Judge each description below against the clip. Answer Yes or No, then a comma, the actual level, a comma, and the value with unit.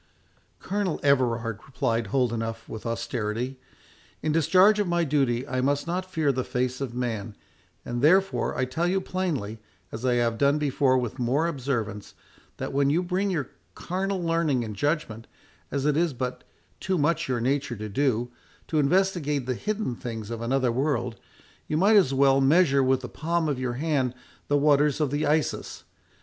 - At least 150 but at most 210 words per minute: Yes, average, 175 wpm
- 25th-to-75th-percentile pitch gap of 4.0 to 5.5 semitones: Yes, average, 4.8 semitones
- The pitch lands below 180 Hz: Yes, low, 135 Hz